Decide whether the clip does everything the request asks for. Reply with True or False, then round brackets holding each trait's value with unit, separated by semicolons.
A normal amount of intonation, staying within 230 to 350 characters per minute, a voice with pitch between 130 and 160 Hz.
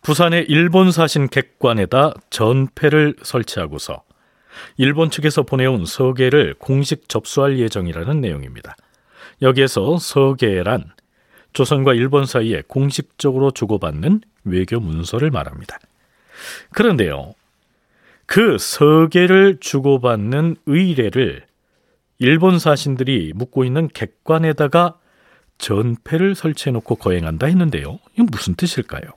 True (5.0 semitones; 270 characters per minute; 140 Hz)